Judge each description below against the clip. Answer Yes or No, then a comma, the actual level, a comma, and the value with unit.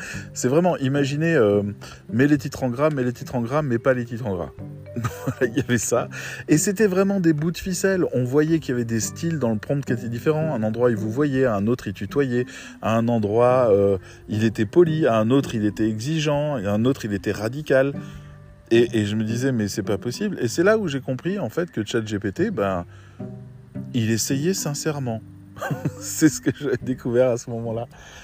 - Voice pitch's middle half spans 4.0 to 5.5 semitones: Yes, average, 5.2 semitones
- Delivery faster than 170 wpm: Yes, fast, 220 wpm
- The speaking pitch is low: Yes, low, 125 Hz